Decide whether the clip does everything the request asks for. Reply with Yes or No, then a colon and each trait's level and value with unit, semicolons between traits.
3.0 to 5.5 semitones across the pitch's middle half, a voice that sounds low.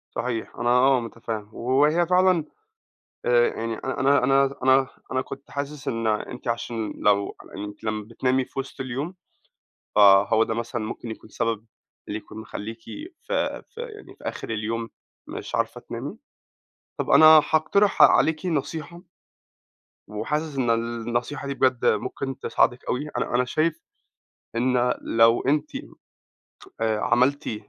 Yes: average, 4.0 semitones; low, 125 Hz